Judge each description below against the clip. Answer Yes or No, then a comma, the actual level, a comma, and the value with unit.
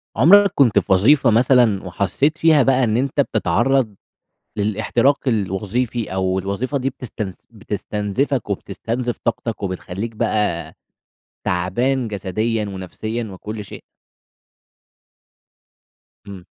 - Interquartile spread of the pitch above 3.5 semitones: Yes, average, 4.4 semitones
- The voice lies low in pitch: Yes, low, 110 Hz